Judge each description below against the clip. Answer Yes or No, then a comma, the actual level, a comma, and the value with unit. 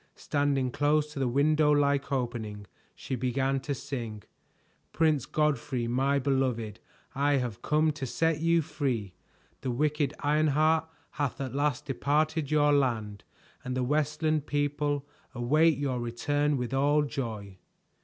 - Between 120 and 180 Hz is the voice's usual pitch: Yes, medium, 140 Hz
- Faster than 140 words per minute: No, slow, 135 wpm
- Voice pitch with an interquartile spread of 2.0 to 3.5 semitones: Yes, average, 3.0 semitones